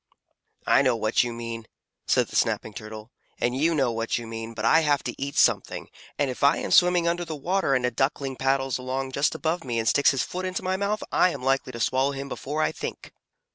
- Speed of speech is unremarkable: No, fast, 235 wpm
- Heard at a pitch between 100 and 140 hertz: Yes, low, 135 Hz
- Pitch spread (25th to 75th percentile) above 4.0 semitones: Yes, average, 4.8 semitones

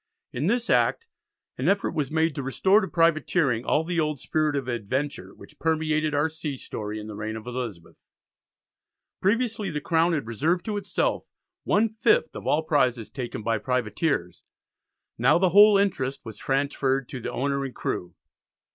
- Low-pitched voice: No, medium, 145 Hz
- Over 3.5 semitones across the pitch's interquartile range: Yes, average, 5.3 semitones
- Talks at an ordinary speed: Yes, average, 170 wpm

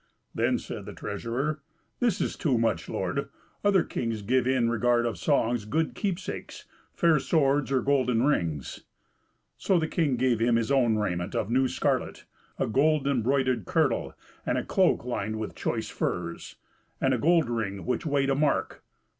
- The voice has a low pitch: Yes, low, 130 Hz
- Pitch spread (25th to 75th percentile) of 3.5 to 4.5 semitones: Yes, average, 4.2 semitones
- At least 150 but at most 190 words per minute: Yes, average, 165 wpm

